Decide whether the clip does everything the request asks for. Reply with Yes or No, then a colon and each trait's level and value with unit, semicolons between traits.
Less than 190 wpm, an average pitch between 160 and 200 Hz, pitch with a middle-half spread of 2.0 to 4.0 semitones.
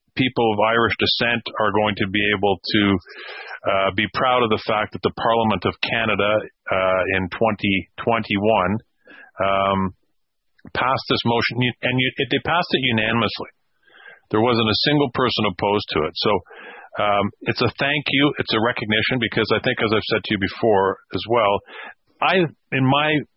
No: average, 170 wpm; low, 110 Hz; average, 3.2 semitones